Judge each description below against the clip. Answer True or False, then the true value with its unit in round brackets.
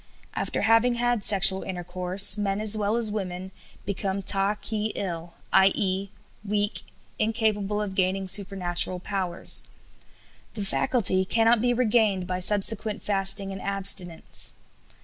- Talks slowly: True (130 wpm)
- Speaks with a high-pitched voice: True (200 Hz)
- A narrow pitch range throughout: True (2.1 semitones)